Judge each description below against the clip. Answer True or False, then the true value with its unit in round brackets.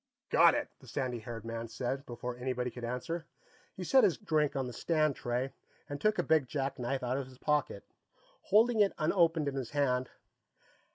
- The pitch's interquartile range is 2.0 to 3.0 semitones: False (4.1 semitones)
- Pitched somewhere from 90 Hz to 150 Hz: True (135 Hz)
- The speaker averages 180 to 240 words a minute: True (185 wpm)